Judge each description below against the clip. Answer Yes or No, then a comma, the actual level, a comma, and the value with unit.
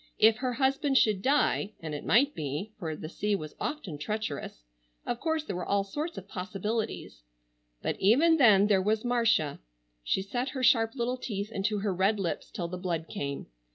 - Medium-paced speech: Yes, average, 175 wpm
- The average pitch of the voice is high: Yes, high, 205 Hz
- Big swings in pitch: Yes, wide, 6.2 semitones